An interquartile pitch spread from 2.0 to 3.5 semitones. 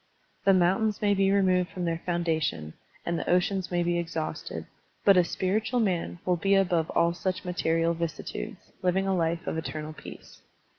Yes: narrow, 2.5 semitones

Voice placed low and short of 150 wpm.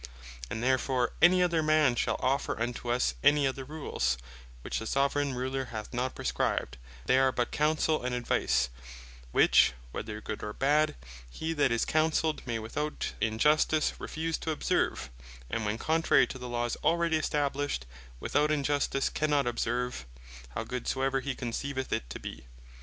No: low, 130 Hz; average, 160 wpm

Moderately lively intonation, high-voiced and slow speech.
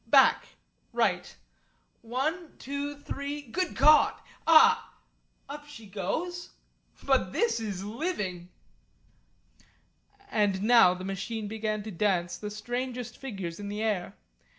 No: wide, 6.1 semitones; high, 225 Hz; slow, 115 wpm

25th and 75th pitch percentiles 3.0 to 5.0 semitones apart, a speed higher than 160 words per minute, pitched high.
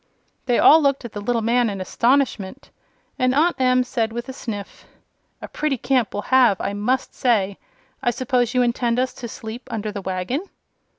Yes: average, 3.3 semitones; average, 185 wpm; high, 240 Hz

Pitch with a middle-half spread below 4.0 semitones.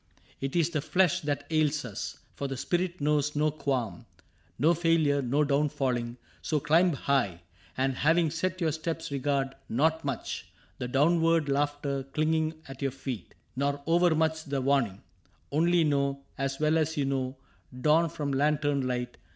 Yes: average, 2.7 semitones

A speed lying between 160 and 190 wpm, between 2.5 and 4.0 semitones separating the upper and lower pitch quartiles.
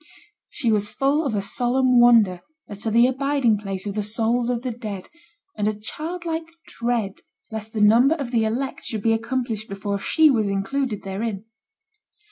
Yes: average, 175 wpm; average, 3.7 semitones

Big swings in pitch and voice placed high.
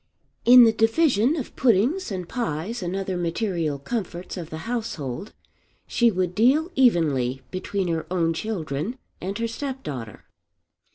Yes: wide, 6.3 semitones; high, 195 Hz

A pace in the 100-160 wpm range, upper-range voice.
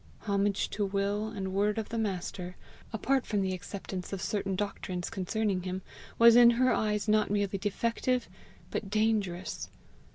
Yes: average, 155 wpm; high, 205 Hz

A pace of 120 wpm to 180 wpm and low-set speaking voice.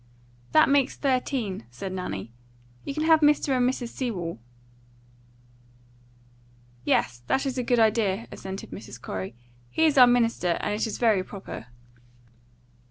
No: average, 140 wpm; high, 230 Hz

